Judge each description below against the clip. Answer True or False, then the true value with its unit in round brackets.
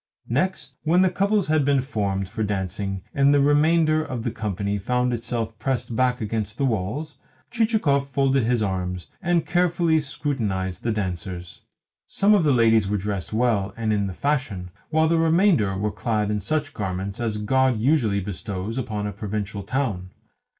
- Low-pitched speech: True (115 Hz)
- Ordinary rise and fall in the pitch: False (6.2 semitones)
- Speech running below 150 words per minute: False (165 wpm)